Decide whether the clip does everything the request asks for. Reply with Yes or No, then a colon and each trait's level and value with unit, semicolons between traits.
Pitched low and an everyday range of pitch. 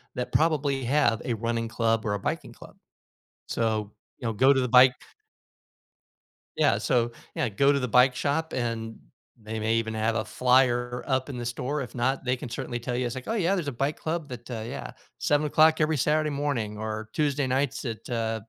Yes: low, 125 Hz; average, 3.6 semitones